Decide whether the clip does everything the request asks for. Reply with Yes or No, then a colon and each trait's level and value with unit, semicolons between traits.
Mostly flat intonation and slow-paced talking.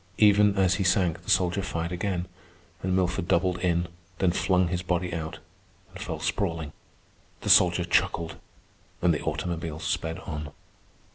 No: narrow, 1.9 semitones; average, 150 wpm